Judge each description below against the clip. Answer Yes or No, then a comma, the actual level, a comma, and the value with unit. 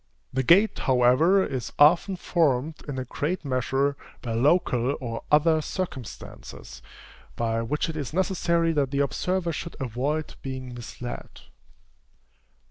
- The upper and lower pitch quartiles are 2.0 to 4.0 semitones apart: No, average, 4.8 semitones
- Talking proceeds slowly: Yes, slow, 130 wpm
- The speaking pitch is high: No, medium, 145 Hz